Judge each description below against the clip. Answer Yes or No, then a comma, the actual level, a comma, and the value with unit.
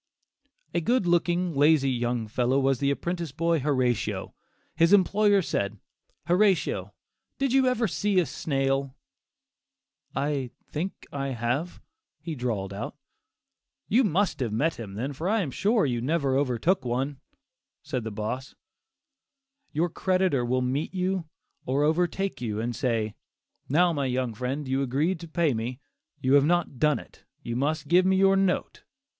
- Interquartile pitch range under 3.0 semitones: No, wide, 5.6 semitones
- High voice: No, medium, 145 Hz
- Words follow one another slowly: No, average, 155 wpm